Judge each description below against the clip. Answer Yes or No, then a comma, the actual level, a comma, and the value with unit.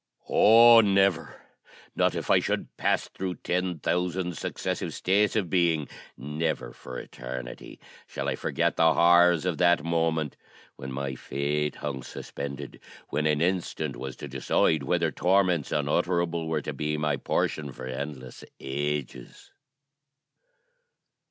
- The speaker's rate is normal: No, slow, 130 wpm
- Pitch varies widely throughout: No, average, 3.8 semitones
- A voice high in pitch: No, very low, 80 Hz